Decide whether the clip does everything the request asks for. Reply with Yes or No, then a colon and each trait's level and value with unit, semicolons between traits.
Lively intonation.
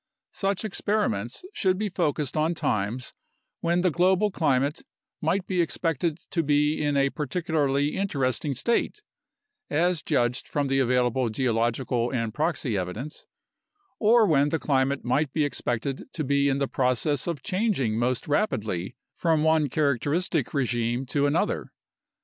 No: average, 4.8 semitones